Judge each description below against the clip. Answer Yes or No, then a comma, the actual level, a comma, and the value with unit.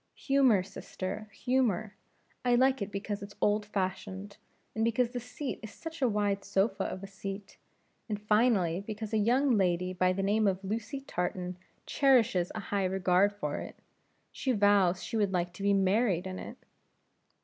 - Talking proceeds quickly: No, average, 170 wpm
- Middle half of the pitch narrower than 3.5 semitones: Yes, average, 3.1 semitones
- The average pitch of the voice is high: Yes, high, 205 Hz